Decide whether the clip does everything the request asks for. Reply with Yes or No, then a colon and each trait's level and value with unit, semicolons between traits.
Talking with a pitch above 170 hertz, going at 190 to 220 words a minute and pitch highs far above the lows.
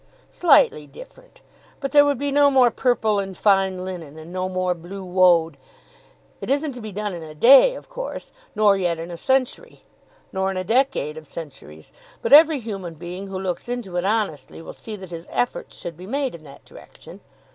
Yes: high, 190 Hz; average, 200 wpm; wide, 6.3 semitones